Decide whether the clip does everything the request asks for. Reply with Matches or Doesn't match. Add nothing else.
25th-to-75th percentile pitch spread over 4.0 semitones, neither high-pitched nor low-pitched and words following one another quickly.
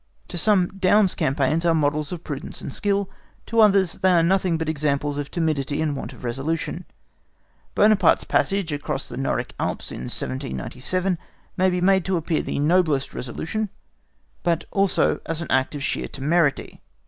Doesn't match